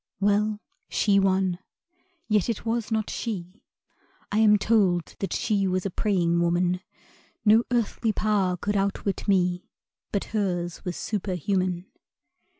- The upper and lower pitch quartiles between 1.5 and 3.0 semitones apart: Yes, average, 2.7 semitones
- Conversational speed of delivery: No, slow, 130 wpm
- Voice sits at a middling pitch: No, high, 195 Hz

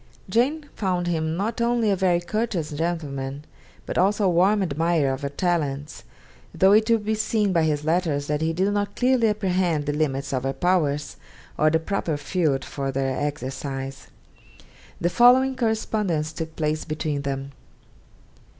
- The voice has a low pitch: No, medium, 165 Hz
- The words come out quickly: No, average, 165 wpm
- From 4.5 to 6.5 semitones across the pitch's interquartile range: Yes, wide, 5.6 semitones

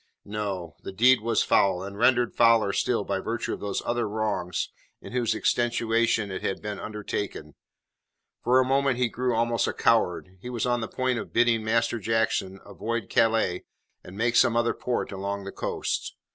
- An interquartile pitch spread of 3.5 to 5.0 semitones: No, average, 3.1 semitones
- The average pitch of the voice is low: Yes, low, 115 Hz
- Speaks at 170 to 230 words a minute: Yes, average, 180 wpm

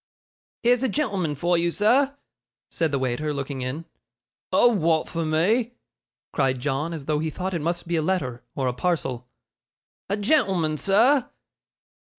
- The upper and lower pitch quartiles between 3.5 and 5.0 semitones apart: No, wide, 5.6 semitones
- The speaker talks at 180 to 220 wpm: No, average, 160 wpm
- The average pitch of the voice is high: No, medium, 165 Hz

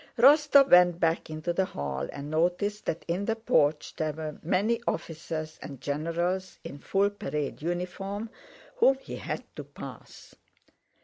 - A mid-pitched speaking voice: Yes, medium, 175 Hz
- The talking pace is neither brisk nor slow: Yes, average, 145 wpm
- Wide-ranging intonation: No, average, 4.5 semitones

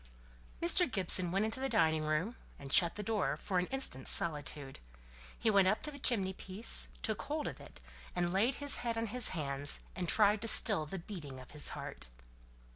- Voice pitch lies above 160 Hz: Yes, high, 190 Hz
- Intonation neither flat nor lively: No, wide, 6.5 semitones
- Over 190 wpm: Yes, average, 200 wpm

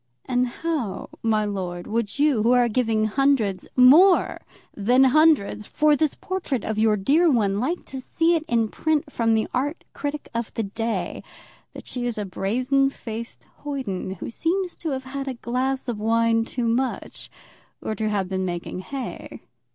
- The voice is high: Yes, high, 240 Hz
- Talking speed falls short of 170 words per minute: No, average, 175 wpm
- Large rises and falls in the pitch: No, average, 4.4 semitones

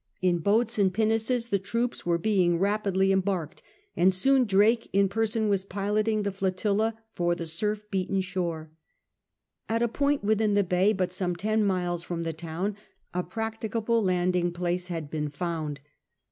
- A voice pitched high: Yes, high, 195 Hz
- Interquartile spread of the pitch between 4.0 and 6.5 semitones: No, average, 3.5 semitones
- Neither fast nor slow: Yes, average, 165 wpm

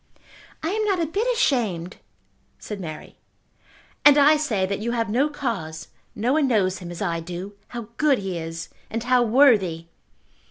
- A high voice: Yes, high, 225 Hz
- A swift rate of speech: No, average, 170 wpm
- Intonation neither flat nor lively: No, wide, 7.7 semitones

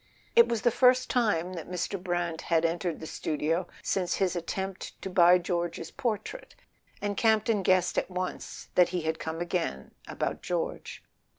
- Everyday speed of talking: Yes, average, 165 wpm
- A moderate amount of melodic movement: Yes, average, 3.1 semitones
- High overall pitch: No, medium, 180 Hz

